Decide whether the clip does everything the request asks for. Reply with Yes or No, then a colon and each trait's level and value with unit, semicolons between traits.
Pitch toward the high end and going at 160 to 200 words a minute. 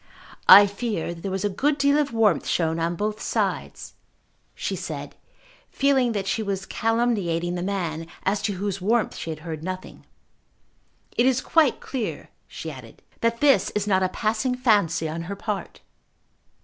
Yes: high, 200 Hz; average, 165 wpm